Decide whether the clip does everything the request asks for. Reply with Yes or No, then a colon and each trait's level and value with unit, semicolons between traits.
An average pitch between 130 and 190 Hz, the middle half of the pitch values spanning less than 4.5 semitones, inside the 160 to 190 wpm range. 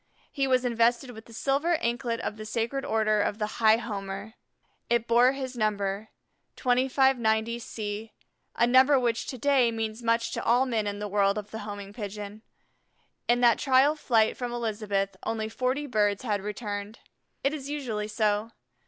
No: high, 230 Hz; average, 3.0 semitones; average, 170 wpm